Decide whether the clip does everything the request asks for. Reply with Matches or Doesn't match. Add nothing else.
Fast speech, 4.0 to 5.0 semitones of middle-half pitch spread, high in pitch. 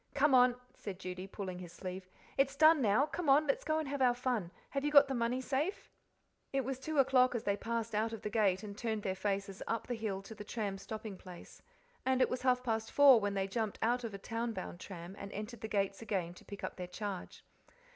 Matches